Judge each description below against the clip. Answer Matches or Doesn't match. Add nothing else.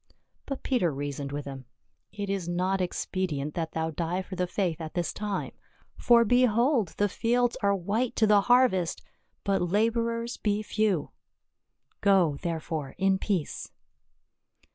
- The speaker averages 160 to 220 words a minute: Doesn't match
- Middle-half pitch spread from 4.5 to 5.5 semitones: Matches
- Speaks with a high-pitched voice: Matches